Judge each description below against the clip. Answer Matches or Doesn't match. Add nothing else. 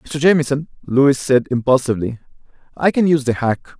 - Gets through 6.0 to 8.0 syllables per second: Matches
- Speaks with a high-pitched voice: Doesn't match